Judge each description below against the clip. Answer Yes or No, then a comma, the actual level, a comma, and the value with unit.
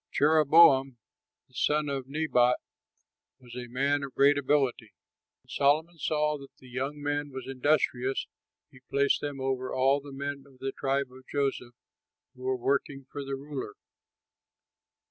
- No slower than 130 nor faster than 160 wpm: Yes, average, 150 wpm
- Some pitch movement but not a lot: No, narrow, 1.8 semitones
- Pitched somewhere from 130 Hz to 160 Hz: Yes, medium, 140 Hz